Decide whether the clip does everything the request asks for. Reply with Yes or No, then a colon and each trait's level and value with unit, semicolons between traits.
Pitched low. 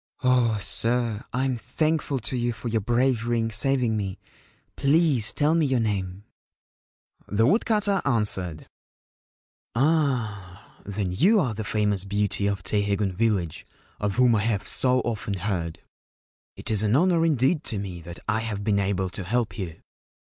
Yes: low, 110 Hz